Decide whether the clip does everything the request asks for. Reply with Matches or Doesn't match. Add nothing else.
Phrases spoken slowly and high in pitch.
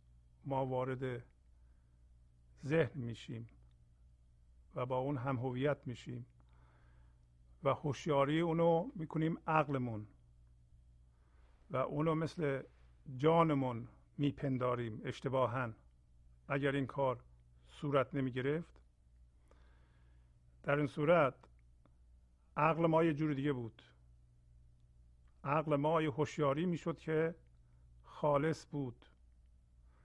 Doesn't match